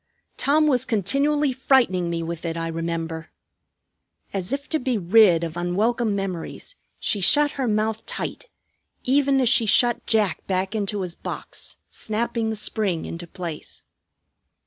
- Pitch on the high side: Yes, high, 215 Hz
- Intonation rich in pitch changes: Yes, wide, 6.4 semitones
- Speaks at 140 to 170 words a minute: Yes, average, 145 wpm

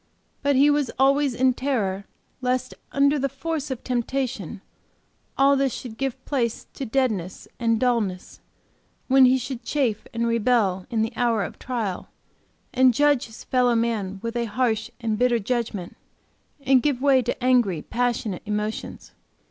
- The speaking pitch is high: Yes, high, 245 Hz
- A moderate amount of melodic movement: Yes, average, 3.1 semitones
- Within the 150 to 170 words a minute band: Yes, average, 155 wpm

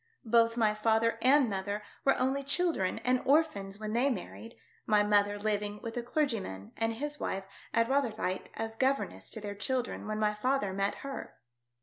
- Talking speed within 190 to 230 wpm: No, average, 175 wpm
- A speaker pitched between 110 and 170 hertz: No, high, 225 Hz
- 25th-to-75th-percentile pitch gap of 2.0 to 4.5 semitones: Yes, average, 4.1 semitones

